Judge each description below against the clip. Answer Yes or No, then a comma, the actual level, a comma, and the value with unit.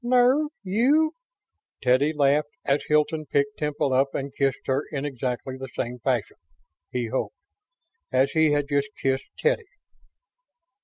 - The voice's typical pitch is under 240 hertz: Yes, medium, 140 Hz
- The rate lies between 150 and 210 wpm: No, average, 140 wpm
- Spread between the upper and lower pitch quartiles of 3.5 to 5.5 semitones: No, average, 2.9 semitones